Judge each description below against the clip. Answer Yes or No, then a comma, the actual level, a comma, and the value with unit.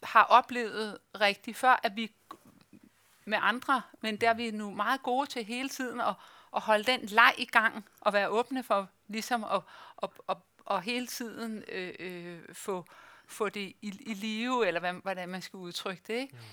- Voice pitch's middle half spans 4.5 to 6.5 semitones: No, average, 3.3 semitones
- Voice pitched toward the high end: Yes, high, 220 Hz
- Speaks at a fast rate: No, average, 190 wpm